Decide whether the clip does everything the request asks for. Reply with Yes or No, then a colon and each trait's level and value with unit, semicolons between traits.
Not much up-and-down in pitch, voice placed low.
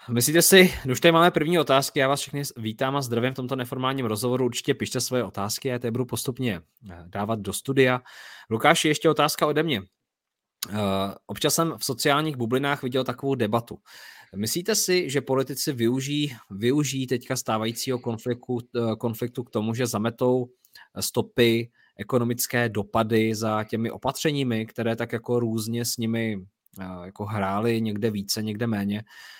No: average, 3.3 semitones; low, 120 Hz